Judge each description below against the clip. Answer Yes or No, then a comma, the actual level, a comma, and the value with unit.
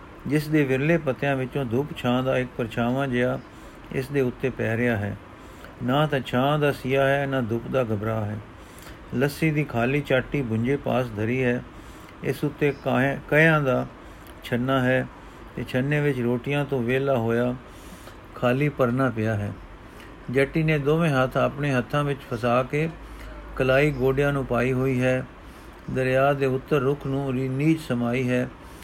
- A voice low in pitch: Yes, low, 130 Hz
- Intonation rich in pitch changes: No, narrow, 2.5 semitones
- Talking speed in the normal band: Yes, average, 155 wpm